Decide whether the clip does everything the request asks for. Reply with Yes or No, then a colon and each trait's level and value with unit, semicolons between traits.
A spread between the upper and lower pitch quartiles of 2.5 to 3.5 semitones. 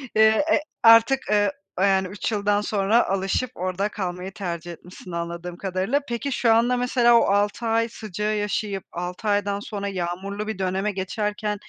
Yes: average, 2.8 semitones